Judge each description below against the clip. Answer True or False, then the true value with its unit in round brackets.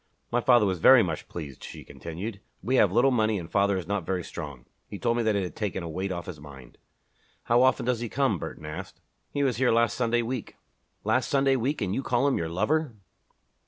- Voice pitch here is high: False (105 Hz)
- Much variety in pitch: True (5.8 semitones)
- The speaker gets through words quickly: True (230 wpm)